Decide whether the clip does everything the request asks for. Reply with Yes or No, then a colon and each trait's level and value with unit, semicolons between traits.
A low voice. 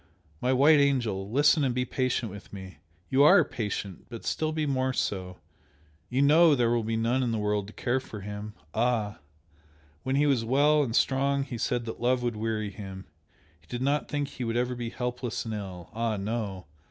Yes: low, 120 Hz